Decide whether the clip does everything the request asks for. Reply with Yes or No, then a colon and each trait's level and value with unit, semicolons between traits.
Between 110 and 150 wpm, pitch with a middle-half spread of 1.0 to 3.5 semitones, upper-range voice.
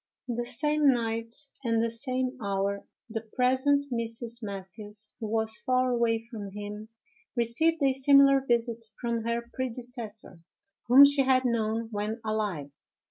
Yes: average, 145 wpm; average, 2.7 semitones; high, 235 Hz